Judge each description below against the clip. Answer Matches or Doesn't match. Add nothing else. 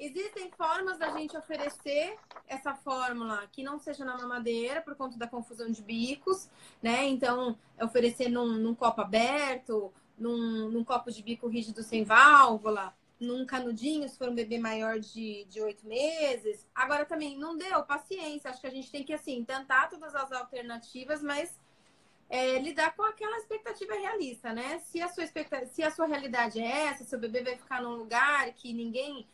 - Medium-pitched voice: Doesn't match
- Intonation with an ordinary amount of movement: Matches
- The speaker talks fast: Doesn't match